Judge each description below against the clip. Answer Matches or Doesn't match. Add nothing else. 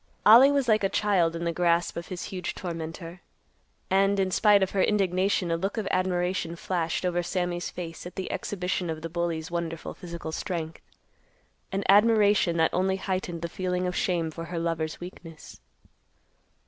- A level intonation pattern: Matches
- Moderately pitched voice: Matches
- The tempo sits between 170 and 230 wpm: Matches